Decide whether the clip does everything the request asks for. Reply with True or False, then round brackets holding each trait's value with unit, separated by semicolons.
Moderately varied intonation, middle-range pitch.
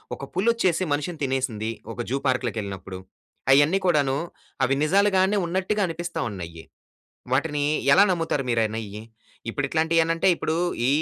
False (6.6 semitones; 145 Hz)